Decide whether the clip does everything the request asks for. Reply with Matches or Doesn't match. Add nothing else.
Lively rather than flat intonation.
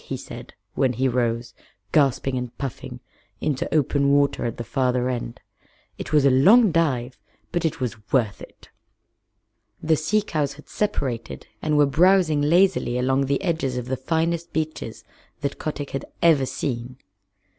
Doesn't match